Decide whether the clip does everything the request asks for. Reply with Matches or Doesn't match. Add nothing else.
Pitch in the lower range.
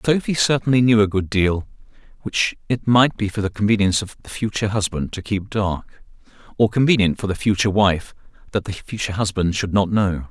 Matches